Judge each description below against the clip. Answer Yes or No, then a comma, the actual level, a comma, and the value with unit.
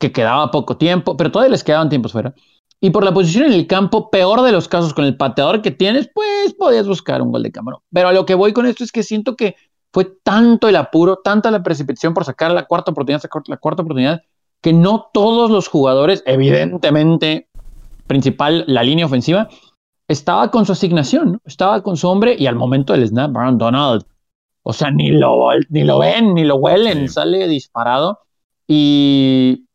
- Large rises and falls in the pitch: Yes, wide, 6.3 semitones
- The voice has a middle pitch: Yes, medium, 170 Hz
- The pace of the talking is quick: Yes, fast, 200 wpm